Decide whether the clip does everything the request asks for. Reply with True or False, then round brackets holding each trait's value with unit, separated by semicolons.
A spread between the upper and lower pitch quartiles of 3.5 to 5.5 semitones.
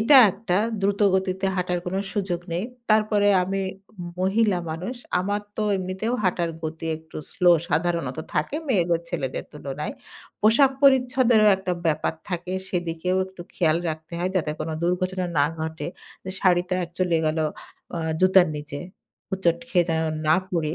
False (3.1 semitones)